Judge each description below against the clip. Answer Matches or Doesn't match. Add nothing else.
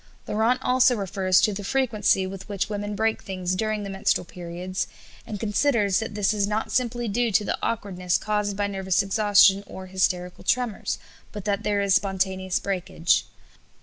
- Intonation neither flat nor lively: Doesn't match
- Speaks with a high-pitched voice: Matches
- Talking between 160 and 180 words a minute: Matches